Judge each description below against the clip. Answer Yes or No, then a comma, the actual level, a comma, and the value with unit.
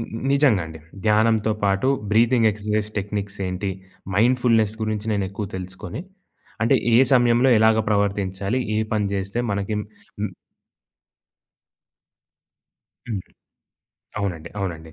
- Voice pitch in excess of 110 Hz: No, low, 105 Hz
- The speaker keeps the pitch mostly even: Yes, narrow, 2.3 semitones